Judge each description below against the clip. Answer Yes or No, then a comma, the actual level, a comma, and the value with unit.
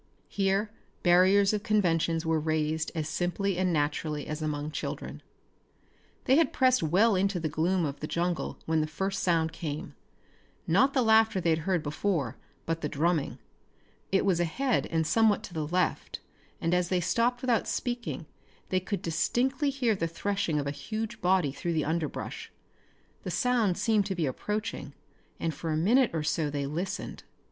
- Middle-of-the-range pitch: Yes, medium, 175 Hz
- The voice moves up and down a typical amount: Yes, average, 4.7 semitones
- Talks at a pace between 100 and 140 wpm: No, average, 170 wpm